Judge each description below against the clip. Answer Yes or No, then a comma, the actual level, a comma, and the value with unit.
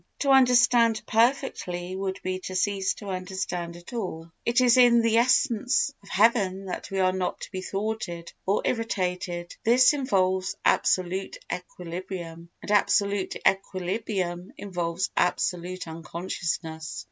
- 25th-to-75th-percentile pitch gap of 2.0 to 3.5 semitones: No, average, 4.1 semitones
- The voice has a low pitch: No, high, 190 Hz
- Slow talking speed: Yes, slow, 130 wpm